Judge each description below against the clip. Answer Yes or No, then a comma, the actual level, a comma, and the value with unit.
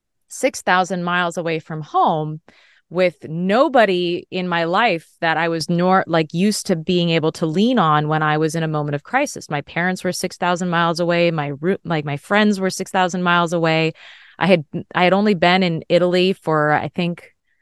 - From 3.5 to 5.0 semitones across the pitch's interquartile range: No, narrow, 2.5 semitones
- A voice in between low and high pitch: Yes, medium, 175 Hz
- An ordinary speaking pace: Yes, average, 185 wpm